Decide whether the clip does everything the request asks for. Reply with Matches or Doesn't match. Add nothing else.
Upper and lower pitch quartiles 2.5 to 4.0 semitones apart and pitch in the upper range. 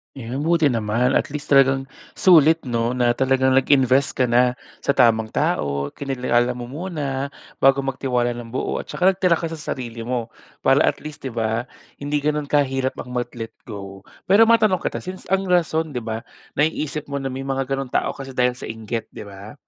Doesn't match